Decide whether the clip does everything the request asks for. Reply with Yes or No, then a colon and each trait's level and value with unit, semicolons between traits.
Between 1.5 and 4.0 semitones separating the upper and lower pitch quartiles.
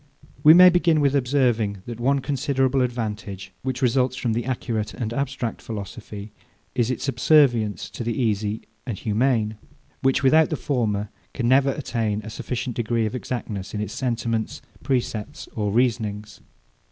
Yes: average, 3.5 semitones